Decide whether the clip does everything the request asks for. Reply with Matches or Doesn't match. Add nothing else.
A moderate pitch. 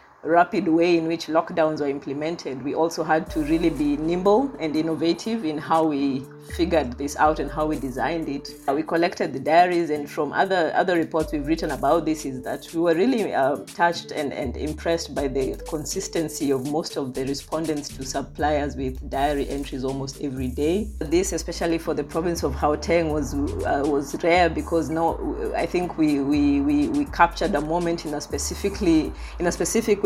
Matches